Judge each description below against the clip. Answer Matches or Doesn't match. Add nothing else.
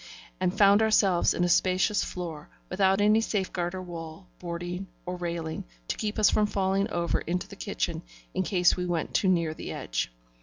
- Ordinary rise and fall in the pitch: Doesn't match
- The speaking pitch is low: Doesn't match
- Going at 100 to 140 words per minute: Doesn't match